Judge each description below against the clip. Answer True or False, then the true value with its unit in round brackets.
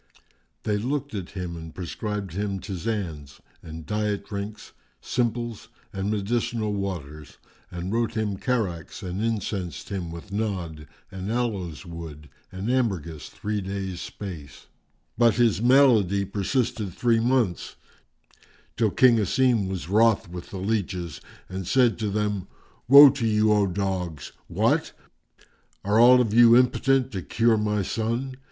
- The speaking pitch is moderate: False (105 Hz)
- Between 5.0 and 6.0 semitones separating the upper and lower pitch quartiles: False (4.0 semitones)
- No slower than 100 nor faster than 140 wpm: True (135 wpm)